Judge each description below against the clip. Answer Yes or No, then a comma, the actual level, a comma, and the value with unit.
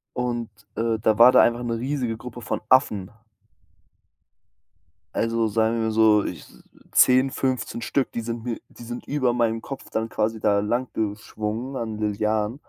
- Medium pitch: No, low, 115 Hz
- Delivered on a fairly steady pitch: Yes, narrow, 2.0 semitones